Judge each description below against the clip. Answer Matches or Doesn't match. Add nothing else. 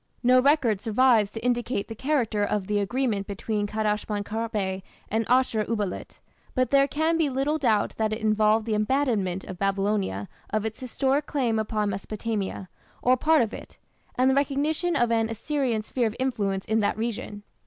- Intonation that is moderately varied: Matches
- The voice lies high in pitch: Matches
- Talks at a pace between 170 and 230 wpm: Matches